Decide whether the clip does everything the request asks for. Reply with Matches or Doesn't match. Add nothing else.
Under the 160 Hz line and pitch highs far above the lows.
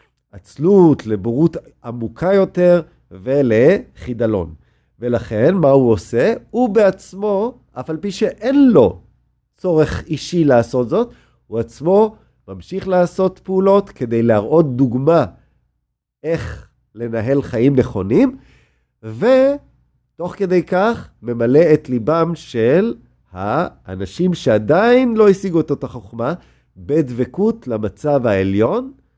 Matches